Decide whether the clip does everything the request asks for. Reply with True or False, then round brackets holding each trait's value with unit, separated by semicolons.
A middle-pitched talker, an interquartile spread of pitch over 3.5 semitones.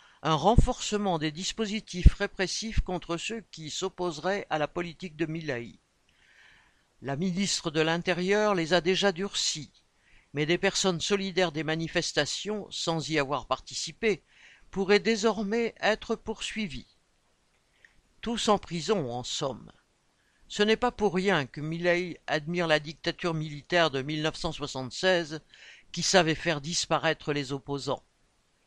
True (175 Hz; 4.3 semitones)